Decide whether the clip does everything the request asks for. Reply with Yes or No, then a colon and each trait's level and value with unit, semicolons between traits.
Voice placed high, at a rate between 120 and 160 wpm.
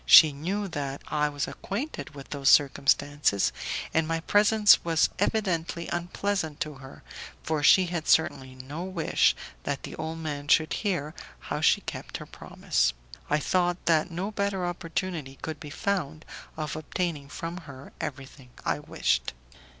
No: medium, 160 Hz; average, 150 wpm